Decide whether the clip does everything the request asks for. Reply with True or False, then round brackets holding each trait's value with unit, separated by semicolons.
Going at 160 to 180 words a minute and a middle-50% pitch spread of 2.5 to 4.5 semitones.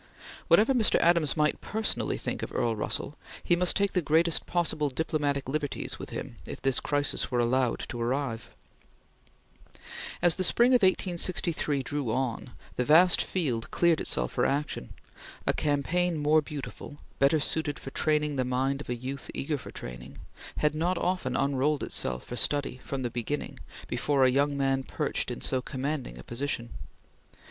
True (165 wpm; 3.7 semitones)